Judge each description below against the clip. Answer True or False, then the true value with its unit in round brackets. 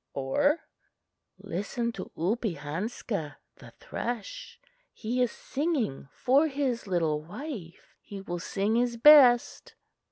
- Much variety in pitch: True (6.3 semitones)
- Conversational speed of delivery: False (105 wpm)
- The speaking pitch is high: True (225 Hz)